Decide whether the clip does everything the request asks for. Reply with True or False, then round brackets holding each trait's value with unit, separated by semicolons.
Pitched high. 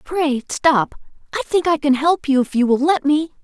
True (295 Hz)